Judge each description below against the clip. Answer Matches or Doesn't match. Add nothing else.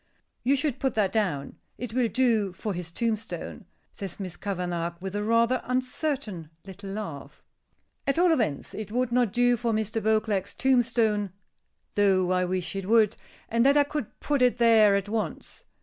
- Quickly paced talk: Doesn't match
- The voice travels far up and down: Doesn't match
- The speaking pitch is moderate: Doesn't match